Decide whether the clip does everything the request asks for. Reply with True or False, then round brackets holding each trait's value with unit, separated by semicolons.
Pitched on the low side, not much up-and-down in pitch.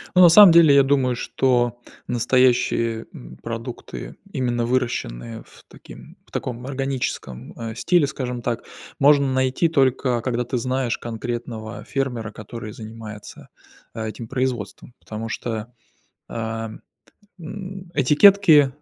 False (125 Hz; 3.0 semitones)